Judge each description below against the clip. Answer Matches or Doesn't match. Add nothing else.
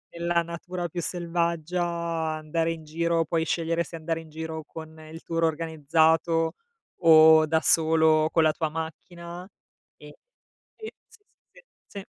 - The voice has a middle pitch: Matches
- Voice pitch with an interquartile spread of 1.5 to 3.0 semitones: Doesn't match